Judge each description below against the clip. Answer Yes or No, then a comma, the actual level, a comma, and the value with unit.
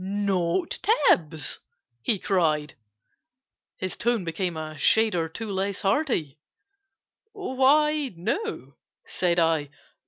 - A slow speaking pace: Yes, slow, 95 wpm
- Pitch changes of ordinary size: No, wide, 7.2 semitones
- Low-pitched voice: No, high, 190 Hz